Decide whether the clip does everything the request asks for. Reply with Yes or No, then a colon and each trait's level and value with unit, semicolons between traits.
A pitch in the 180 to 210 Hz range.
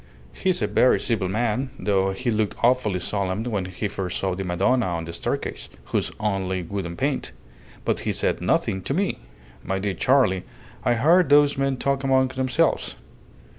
No: low, 105 Hz